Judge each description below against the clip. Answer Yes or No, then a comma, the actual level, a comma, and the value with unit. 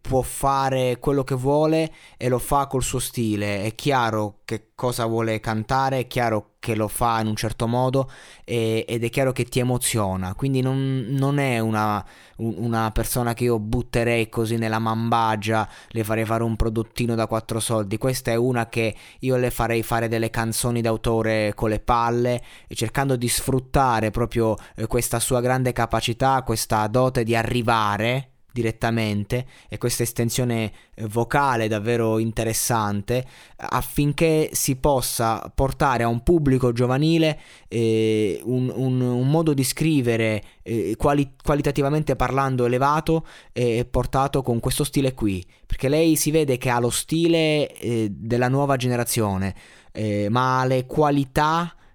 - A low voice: Yes, low, 120 Hz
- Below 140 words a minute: No, average, 150 wpm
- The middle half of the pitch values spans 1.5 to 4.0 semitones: Yes, average, 2.9 semitones